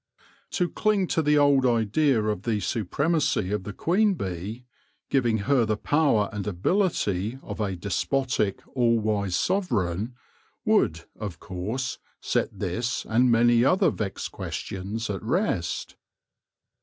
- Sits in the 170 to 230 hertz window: No, low, 115 Hz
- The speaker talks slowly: Yes, slow, 130 wpm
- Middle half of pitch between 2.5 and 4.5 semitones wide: No, wide, 5.6 semitones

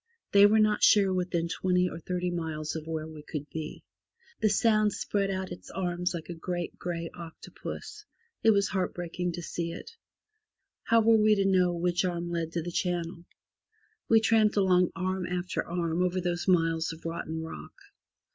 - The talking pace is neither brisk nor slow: Yes, average, 180 wpm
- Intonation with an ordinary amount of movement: No, narrow, 2.3 semitones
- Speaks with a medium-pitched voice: Yes, medium, 180 Hz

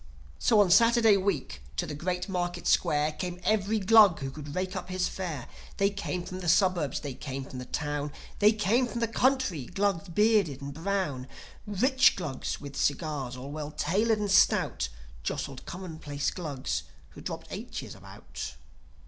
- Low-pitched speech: No, medium, 180 Hz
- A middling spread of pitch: No, wide, 5.7 semitones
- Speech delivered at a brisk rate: No, average, 165 wpm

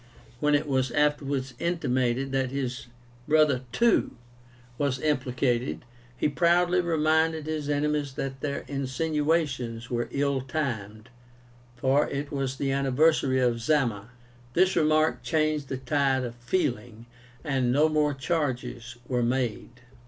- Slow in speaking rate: Yes, slow, 125 wpm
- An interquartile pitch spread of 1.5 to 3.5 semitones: Yes, average, 3.2 semitones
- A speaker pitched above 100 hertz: Yes, medium, 140 Hz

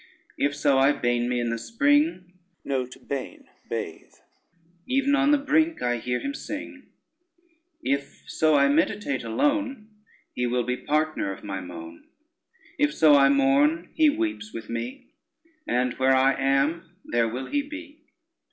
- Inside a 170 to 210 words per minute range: No, average, 145 wpm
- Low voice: No, medium, 145 Hz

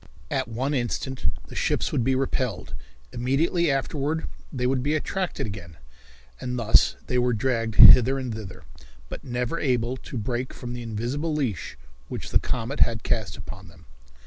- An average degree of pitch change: Yes, average, 3.2 semitones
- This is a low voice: Yes, low, 125 Hz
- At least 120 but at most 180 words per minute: Yes, average, 165 wpm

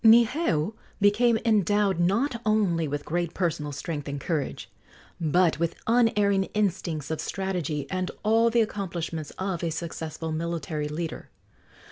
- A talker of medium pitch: Yes, medium, 175 Hz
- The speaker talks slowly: Yes, slow, 130 wpm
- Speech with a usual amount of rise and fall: Yes, average, 4.7 semitones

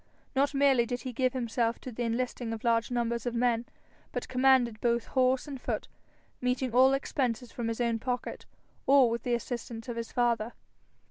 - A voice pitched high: Yes, high, 245 Hz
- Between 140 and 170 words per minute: No, average, 190 wpm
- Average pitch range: No, narrow, 1.7 semitones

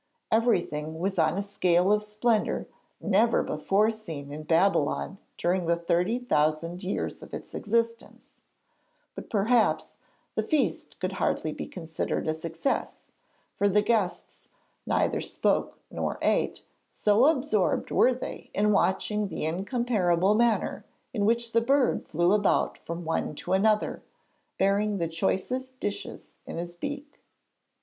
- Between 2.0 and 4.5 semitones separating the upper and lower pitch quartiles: No, average, 4.9 semitones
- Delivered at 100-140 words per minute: Yes, slow, 135 wpm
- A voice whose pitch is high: Yes, high, 200 Hz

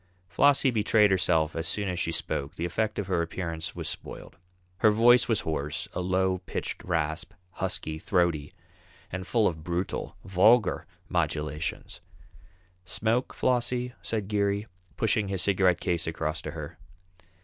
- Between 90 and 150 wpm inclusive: Yes, average, 145 wpm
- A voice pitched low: Yes, very low, 95 Hz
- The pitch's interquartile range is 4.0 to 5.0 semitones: Yes, average, 4.5 semitones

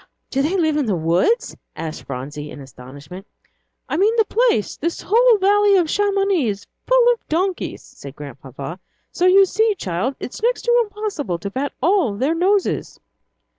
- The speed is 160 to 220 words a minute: Yes, average, 170 wpm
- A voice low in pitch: No, very high, 330 Hz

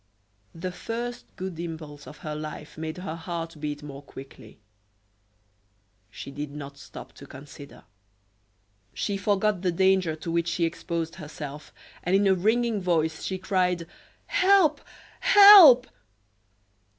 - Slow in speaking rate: Yes, slow, 130 wpm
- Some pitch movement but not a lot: Yes, average, 4.3 semitones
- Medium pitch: Yes, medium, 170 Hz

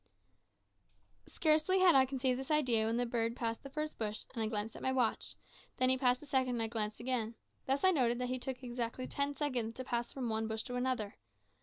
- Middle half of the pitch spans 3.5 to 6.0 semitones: No, average, 2.7 semitones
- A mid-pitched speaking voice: No, very high, 250 Hz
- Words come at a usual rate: No, fast, 230 wpm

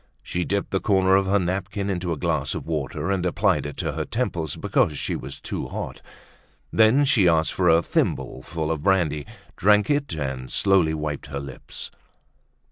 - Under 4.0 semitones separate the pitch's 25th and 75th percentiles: No, average, 4.4 semitones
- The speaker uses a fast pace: No, average, 180 wpm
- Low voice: Yes, very low, 85 Hz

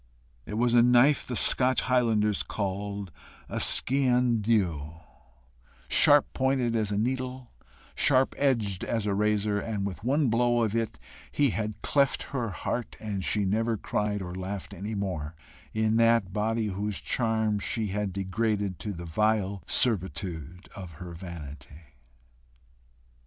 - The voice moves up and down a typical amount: Yes, average, 3.3 semitones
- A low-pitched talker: Yes, low, 105 Hz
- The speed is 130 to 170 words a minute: Yes, average, 140 wpm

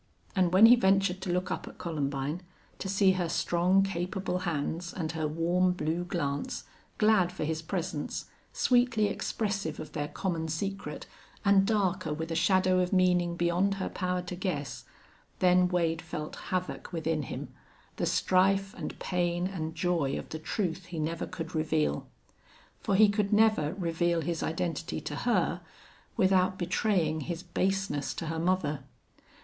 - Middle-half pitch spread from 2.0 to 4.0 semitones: Yes, average, 2.8 semitones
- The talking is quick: No, average, 155 wpm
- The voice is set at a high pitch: No, medium, 175 Hz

